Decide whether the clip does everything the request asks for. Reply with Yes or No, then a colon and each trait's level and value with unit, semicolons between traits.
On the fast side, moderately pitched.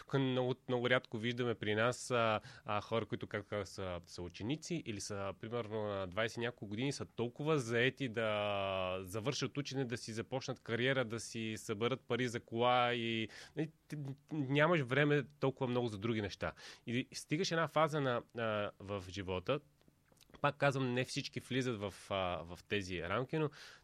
No: fast, 170 wpm; low, 120 Hz